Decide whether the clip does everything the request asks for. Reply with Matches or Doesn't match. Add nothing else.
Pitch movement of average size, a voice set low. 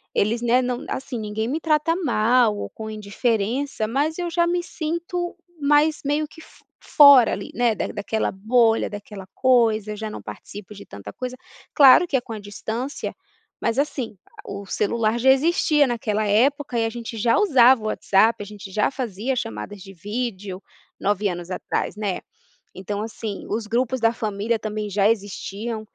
Doesn't match